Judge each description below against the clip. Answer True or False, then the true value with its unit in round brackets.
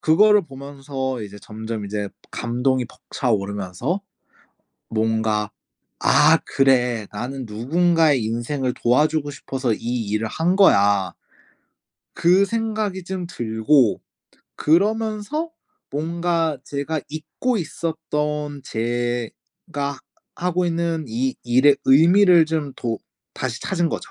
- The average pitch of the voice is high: False (140 Hz)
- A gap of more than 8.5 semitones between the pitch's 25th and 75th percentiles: False (6.2 semitones)